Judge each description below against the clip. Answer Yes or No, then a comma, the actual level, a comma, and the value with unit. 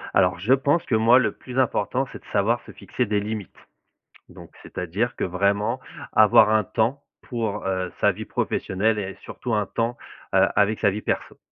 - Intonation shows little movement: No, average, 3.1 semitones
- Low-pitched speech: Yes, low, 110 Hz